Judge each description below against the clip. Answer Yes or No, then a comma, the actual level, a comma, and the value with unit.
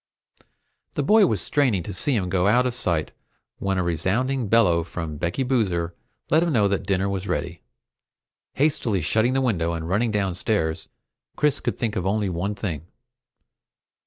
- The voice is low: Yes, low, 100 Hz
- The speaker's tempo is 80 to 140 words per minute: No, average, 160 wpm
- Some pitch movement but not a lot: No, wide, 5.7 semitones